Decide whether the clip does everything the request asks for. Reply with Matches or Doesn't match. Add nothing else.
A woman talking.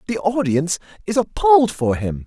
Doesn't match